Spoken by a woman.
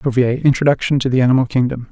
No: male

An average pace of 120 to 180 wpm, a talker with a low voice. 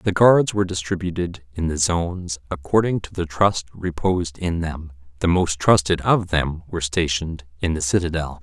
Yes: average, 170 wpm; very low, 85 Hz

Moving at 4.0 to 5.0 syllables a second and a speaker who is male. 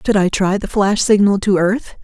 No: 4.8 syllables/s; female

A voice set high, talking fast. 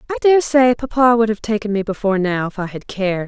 Yes: high, 220 Hz; fast, 255 wpm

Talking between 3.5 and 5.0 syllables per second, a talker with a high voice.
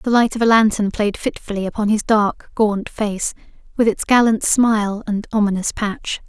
Yes: 4.8 syllables/s; high, 215 Hz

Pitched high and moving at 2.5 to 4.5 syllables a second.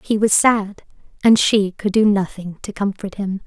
Yes: high, 200 Hz; 4.4 syllables/s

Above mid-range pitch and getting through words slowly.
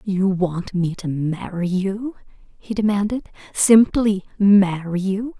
Yes: high, 195 Hz; slow, 110 wpm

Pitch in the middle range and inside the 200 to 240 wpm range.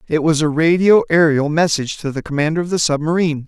Yes: medium, 155 Hz; fast, 205 wpm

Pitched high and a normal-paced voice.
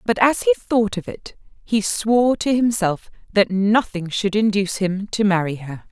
Yes: high, 205 Hz; average, 180 wpm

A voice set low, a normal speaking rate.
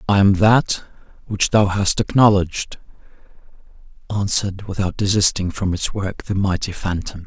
No: very low, 95 Hz; slow, 130 wpm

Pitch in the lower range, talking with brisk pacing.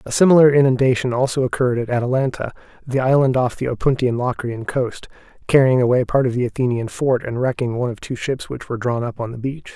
Yes: low, 125 Hz; fast, 210 wpm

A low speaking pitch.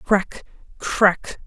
No: high, 195 Hz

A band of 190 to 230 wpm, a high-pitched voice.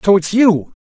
Yes: fast, 215 wpm; high, 195 Hz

